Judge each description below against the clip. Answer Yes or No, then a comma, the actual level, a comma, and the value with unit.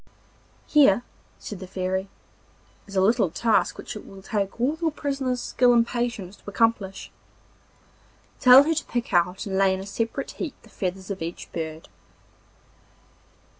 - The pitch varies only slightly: No, average, 4.4 semitones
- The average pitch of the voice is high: Yes, high, 205 Hz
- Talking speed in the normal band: Yes, average, 160 wpm